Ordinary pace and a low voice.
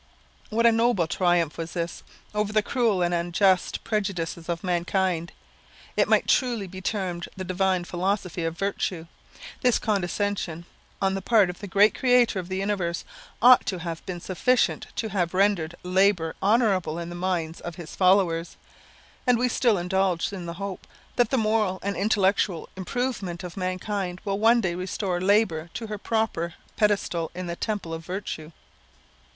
No: average, 165 wpm; high, 190 Hz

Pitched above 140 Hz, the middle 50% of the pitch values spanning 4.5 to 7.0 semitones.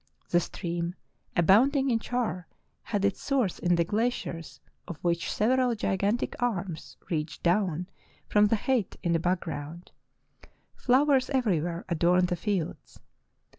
Yes: medium, 185 Hz; wide, 5.5 semitones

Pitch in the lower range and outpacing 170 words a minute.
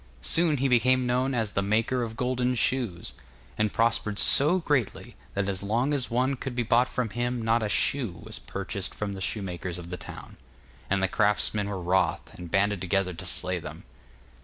Yes: low, 110 Hz; average, 190 wpm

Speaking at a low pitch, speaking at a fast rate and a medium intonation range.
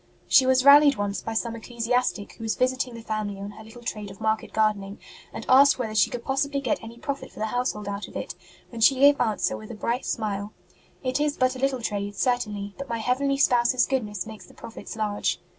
No: high, 230 Hz; fast, 225 wpm; average, 3.4 semitones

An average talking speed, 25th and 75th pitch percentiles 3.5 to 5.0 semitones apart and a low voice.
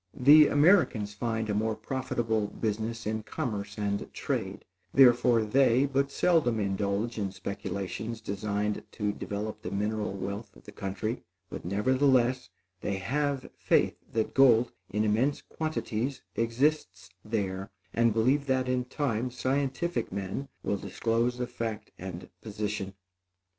No: slow, 130 wpm; average, 4.0 semitones; low, 110 Hz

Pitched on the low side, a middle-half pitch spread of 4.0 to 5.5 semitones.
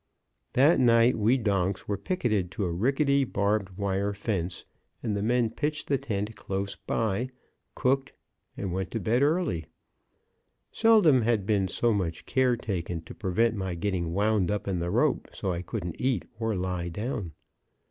Yes: low, 105 Hz; average, 4.4 semitones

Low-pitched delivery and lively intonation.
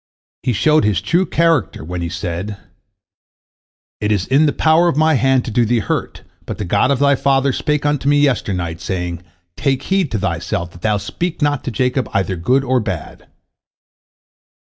Yes: low, 125 Hz; wide, 7.2 semitones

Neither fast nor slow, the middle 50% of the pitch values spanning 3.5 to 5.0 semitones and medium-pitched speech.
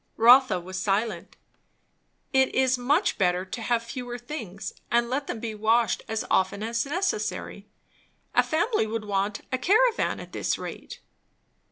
No: average, 150 wpm; average, 3.9 semitones; high, 230 Hz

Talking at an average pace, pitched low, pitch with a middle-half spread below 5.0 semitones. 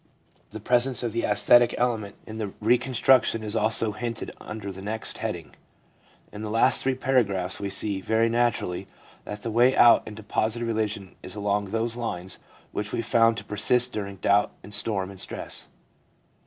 Yes: average, 170 wpm; low, 110 Hz; narrow, 2.5 semitones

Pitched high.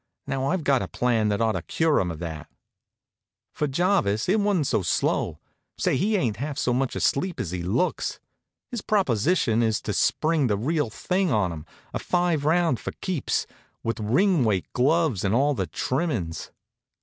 No: low, 130 Hz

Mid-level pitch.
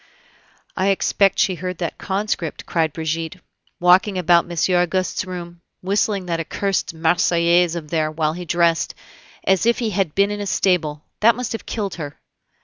Yes: medium, 180 Hz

